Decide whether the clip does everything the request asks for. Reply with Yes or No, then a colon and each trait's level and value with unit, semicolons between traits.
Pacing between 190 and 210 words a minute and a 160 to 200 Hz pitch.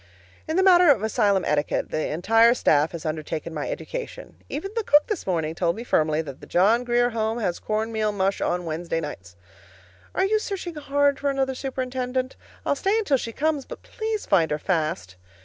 No: average, 195 wpm; high, 225 Hz